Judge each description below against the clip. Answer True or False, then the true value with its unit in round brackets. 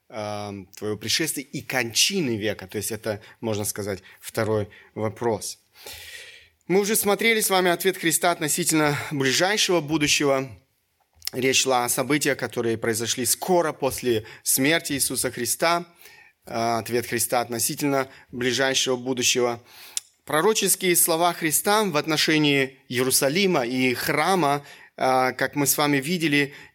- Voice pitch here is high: False (135 Hz)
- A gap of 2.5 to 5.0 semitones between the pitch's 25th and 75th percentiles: False (5.4 semitones)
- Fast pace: False (115 wpm)